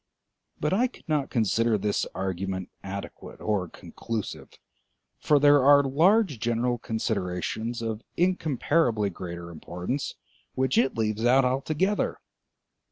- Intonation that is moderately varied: No, wide, 6.2 semitones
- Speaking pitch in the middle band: No, low, 115 Hz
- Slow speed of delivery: Yes, slow, 115 wpm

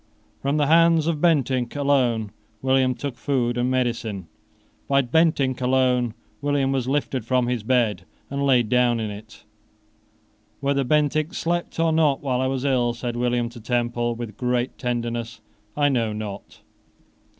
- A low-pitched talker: Yes, low, 125 Hz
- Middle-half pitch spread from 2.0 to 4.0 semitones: Yes, average, 2.8 semitones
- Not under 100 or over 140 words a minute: No, average, 150 wpm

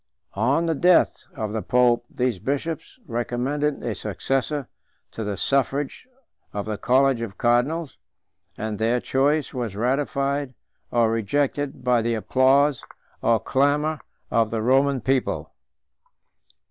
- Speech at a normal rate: No, slow, 130 wpm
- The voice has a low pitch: Yes, low, 130 Hz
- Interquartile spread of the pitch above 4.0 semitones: No, average, 3.7 semitones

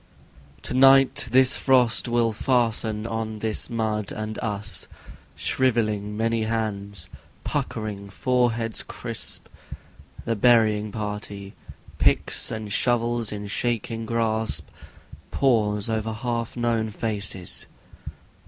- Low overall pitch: Yes, low, 110 Hz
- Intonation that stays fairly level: Yes, narrow, 2.0 semitones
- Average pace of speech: No, slow, 105 wpm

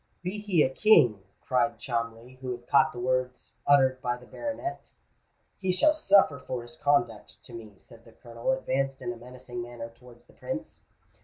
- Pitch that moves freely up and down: No, average, 3.3 semitones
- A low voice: Yes, low, 125 Hz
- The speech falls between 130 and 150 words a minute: No, average, 175 wpm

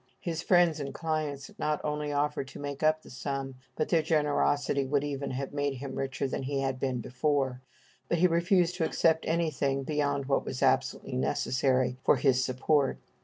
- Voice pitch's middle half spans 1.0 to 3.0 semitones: Yes, narrow, 2.4 semitones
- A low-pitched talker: No, medium, 145 Hz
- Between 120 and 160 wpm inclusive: No, average, 180 wpm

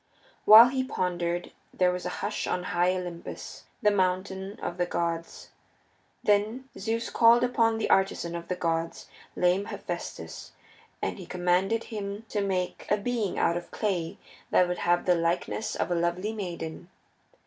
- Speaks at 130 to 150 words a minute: No, average, 160 wpm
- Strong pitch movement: No, average, 3.2 semitones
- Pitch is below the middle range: No, medium, 185 Hz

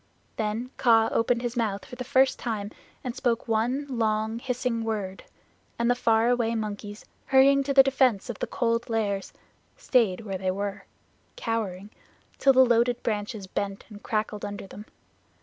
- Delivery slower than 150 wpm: No, average, 165 wpm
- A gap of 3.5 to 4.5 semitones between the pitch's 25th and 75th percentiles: No, average, 3.0 semitones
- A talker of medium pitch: No, high, 225 Hz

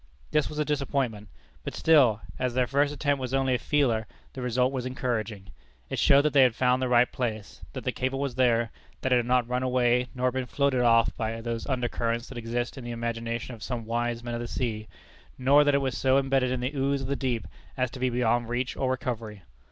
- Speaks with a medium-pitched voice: No, low, 125 Hz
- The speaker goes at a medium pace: No, fast, 235 wpm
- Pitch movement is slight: Yes, narrow, 2.2 semitones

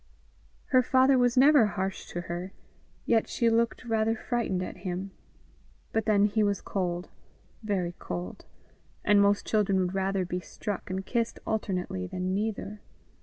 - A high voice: Yes, high, 200 Hz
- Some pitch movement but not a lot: Yes, average, 3.5 semitones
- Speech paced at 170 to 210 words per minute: No, average, 150 wpm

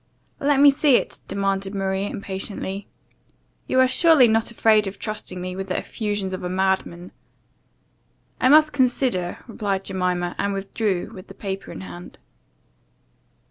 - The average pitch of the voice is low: No, high, 195 Hz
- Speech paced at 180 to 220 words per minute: No, average, 150 wpm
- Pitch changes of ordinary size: Yes, average, 3.5 semitones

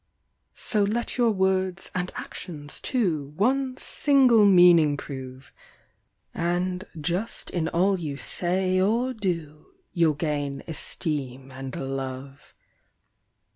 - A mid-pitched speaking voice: Yes, medium, 175 Hz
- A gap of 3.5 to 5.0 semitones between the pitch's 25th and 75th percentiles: No, wide, 5.4 semitones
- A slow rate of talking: Yes, slow, 105 wpm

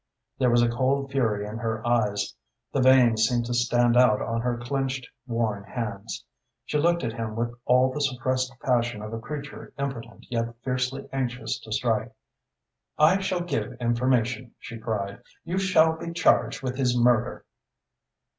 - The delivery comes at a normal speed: Yes, average, 165 wpm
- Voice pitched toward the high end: No, low, 120 Hz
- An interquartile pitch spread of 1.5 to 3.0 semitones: Yes, narrow, 2.5 semitones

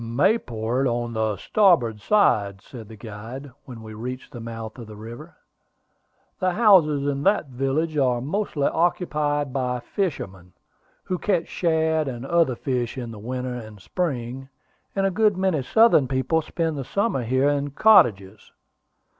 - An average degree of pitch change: No, wide, 5.7 semitones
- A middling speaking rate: Yes, average, 155 wpm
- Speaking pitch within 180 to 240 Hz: No, low, 135 Hz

